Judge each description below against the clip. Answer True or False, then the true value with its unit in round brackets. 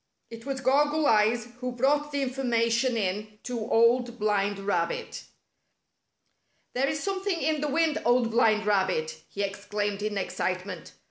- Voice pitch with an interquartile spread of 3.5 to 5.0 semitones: True (4.7 semitones)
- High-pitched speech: True (230 Hz)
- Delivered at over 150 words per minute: False (145 wpm)